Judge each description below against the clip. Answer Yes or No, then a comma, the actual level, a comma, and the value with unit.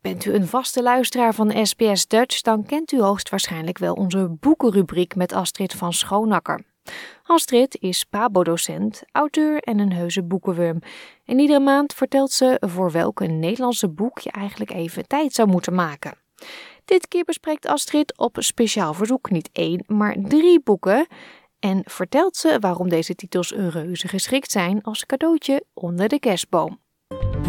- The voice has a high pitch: Yes, high, 210 Hz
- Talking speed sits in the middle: Yes, average, 155 wpm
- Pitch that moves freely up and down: Yes, wide, 6.5 semitones